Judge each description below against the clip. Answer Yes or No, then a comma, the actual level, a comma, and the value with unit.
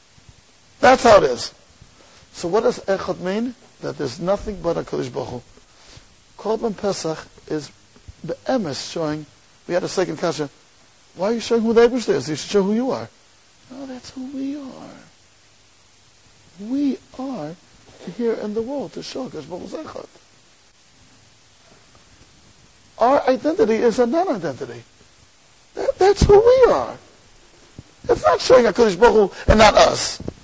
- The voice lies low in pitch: No, high, 210 Hz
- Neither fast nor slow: Yes, average, 150 wpm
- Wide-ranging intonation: Yes, wide, 9.0 semitones